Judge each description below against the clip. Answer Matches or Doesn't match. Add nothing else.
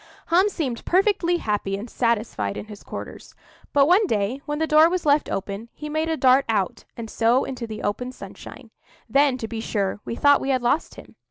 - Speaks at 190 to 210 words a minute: Matches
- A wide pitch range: Matches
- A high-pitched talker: Matches